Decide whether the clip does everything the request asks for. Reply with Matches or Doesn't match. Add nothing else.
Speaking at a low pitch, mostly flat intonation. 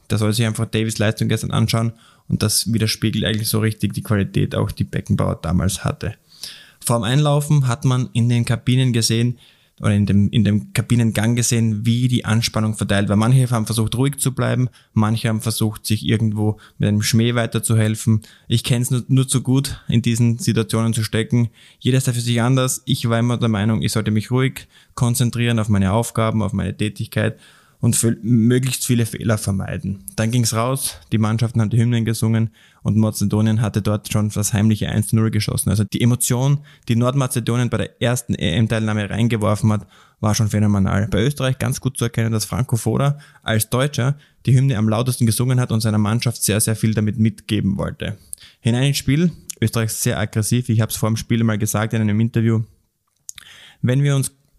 Matches